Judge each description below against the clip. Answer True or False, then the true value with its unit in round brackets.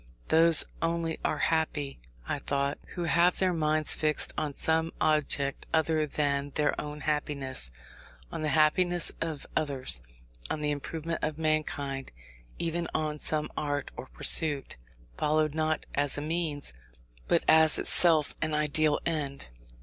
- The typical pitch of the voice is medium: True (155 Hz)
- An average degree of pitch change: False (1.8 semitones)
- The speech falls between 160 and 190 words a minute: False (140 wpm)